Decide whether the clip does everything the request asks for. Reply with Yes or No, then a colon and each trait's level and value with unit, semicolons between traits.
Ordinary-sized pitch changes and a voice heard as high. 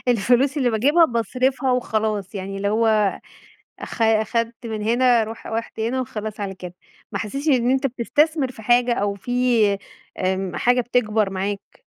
Yes: average, 3.1 semitones; high, 230 Hz